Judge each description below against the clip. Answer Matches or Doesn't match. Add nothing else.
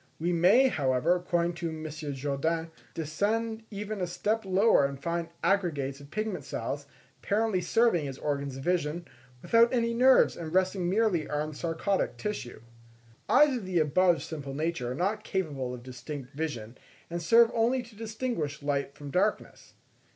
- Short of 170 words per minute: Matches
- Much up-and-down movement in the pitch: Matches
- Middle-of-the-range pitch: Matches